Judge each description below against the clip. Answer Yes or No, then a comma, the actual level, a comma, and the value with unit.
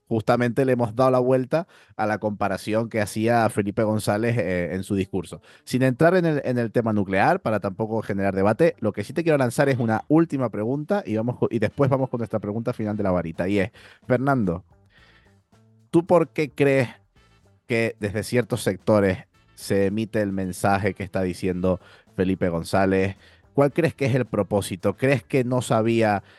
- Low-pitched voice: Yes, low, 110 Hz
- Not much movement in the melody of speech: No, average, 4.2 semitones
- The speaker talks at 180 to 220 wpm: Yes, average, 185 wpm